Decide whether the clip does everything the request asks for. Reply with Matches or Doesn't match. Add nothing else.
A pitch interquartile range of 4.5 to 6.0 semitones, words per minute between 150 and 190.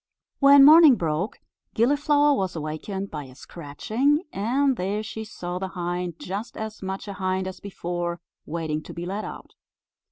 Matches